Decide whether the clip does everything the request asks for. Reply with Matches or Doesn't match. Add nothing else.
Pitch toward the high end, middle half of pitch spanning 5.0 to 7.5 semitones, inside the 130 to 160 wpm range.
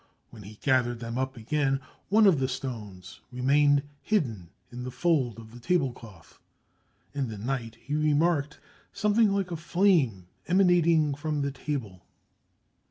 Doesn't match